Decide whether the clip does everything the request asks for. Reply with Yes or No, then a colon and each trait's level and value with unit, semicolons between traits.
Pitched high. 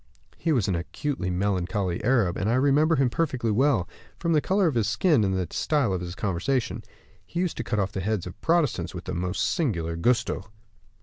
No: low, 110 Hz